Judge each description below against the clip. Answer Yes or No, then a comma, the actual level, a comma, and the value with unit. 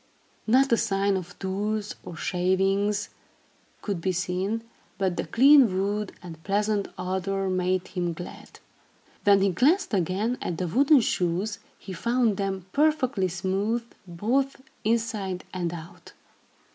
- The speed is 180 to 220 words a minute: No, slow, 135 wpm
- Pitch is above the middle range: Yes, high, 195 Hz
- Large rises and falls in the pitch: No, average, 3.3 semitones